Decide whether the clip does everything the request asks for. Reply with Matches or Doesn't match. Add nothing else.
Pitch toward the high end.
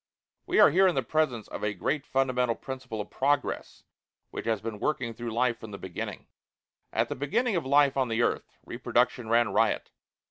Doesn't match